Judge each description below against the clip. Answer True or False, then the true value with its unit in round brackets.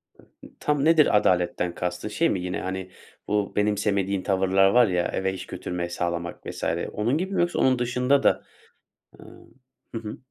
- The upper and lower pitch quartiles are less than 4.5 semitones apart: False (5.2 semitones)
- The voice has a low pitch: True (100 Hz)